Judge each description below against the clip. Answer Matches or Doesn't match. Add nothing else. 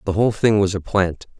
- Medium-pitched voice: Doesn't match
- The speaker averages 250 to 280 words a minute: Matches